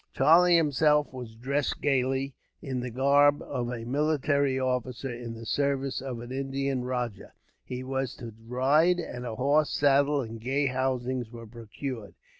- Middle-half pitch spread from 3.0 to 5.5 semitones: No, narrow, 2.4 semitones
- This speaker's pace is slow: No, average, 155 wpm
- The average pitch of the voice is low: Yes, low, 130 Hz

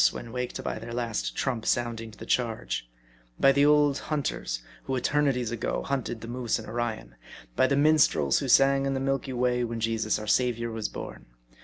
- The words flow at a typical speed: Yes, average, 190 wpm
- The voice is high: No, low, 120 Hz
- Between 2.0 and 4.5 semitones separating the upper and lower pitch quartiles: Yes, average, 3.2 semitones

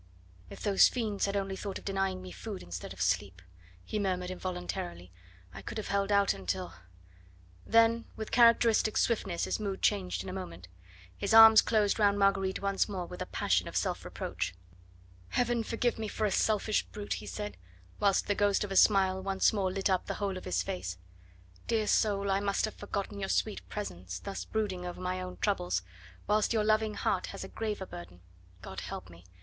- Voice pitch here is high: Yes, high, 195 Hz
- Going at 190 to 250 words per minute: Yes, average, 195 wpm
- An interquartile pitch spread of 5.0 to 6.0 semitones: No, average, 3.4 semitones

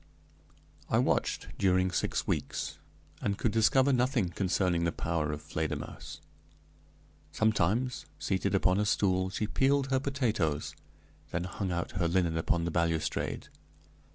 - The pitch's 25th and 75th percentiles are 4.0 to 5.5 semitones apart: Yes, average, 4.8 semitones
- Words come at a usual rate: No, slow, 130 wpm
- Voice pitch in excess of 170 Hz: No, very low, 95 Hz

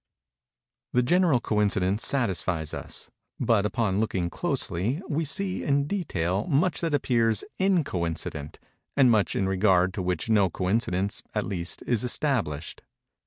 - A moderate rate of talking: No, slow, 130 wpm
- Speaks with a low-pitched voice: Yes, low, 105 Hz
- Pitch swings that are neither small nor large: No, wide, 6.9 semitones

